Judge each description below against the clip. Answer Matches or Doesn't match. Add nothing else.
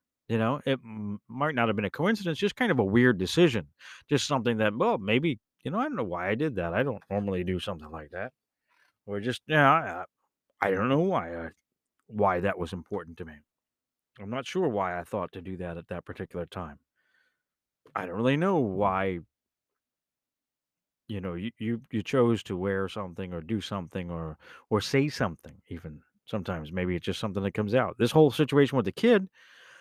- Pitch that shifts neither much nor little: Doesn't match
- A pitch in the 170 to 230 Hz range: Doesn't match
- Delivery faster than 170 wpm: Matches